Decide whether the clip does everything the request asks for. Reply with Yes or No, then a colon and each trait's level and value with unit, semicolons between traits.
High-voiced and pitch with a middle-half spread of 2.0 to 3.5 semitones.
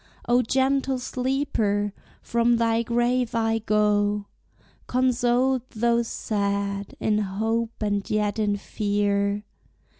Yes: high, 225 Hz; average, 2.8 semitones